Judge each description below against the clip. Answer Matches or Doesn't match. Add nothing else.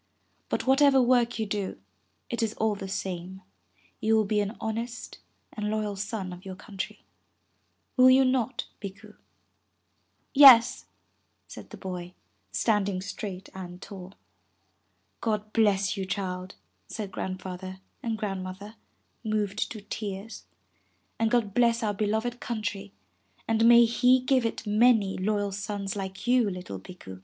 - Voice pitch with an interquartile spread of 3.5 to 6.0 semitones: Doesn't match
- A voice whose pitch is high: Matches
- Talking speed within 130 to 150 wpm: Matches